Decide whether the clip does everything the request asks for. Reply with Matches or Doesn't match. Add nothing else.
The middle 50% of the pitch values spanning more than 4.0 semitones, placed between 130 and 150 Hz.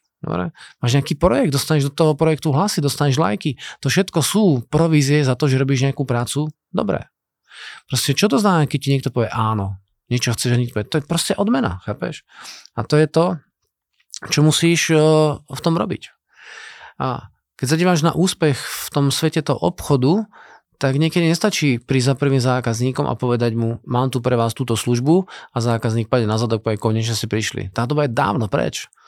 Matches